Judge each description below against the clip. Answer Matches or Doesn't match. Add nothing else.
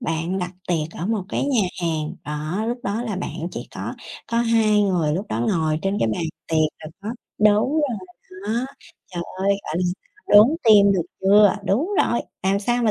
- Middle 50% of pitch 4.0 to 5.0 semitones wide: Matches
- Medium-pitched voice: Doesn't match